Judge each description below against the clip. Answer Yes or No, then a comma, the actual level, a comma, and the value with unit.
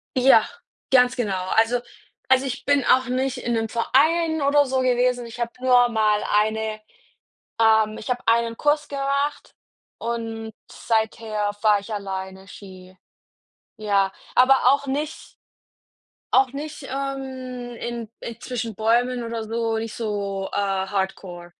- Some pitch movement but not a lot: Yes, average, 3.2 semitones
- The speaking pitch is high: Yes, high, 235 Hz